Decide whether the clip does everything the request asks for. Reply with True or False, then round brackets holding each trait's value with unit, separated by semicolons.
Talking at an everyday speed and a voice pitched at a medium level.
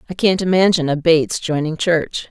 True (180 wpm; 165 Hz)